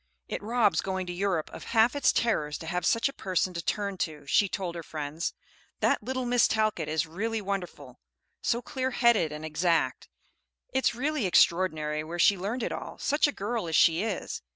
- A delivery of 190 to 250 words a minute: Yes, average, 195 wpm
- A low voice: No, high, 190 Hz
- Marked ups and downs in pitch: Yes, wide, 6.0 semitones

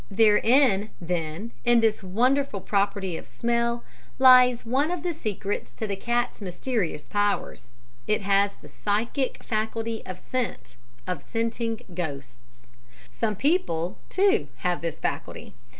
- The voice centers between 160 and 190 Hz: No, high, 215 Hz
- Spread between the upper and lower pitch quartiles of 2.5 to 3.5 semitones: No, average, 4.6 semitones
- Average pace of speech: No, slow, 130 wpm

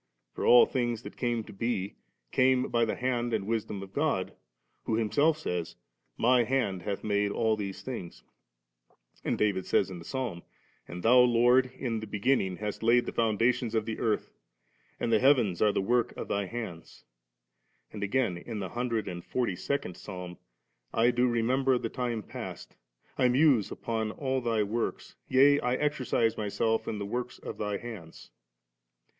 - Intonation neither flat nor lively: Yes, average, 3.5 semitones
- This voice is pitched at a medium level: No, low, 115 Hz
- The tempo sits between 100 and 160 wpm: No, average, 175 wpm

